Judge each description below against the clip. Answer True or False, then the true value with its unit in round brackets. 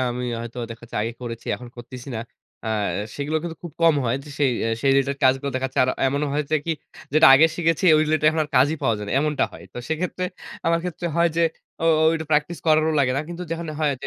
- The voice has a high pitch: False (150 Hz)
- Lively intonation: False (3.9 semitones)